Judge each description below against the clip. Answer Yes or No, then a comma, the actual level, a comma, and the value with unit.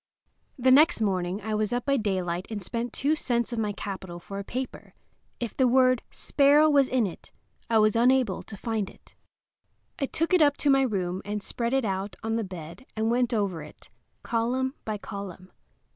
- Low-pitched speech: No, high, 225 Hz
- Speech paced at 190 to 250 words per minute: Yes, average, 195 wpm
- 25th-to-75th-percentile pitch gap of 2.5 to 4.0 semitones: No, average, 4.6 semitones